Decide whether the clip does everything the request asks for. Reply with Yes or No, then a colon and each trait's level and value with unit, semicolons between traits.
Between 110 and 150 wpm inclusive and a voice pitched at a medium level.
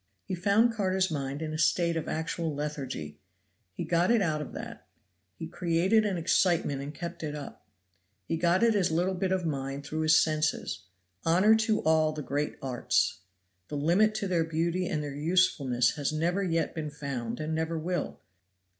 No: average, 180 wpm; medium, 160 Hz